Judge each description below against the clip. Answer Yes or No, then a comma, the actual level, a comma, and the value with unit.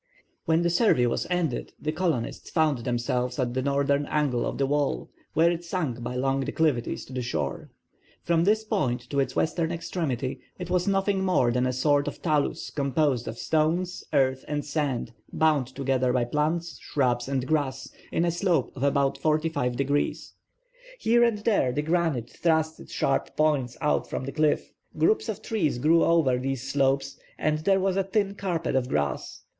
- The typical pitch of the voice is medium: Yes, medium, 145 Hz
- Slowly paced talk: No, average, 180 wpm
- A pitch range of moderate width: Yes, average, 4.5 semitones